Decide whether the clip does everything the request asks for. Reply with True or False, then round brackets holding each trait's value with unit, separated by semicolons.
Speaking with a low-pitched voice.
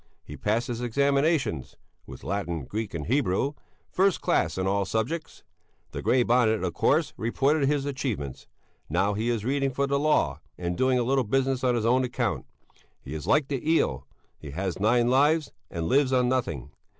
True (125 Hz)